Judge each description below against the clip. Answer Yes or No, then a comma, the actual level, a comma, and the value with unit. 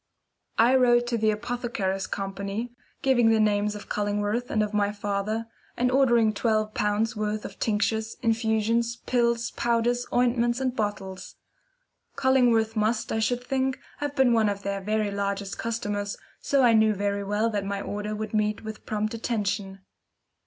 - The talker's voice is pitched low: No, high, 220 Hz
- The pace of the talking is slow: No, average, 160 wpm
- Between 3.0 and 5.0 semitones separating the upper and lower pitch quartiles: No, narrow, 2.5 semitones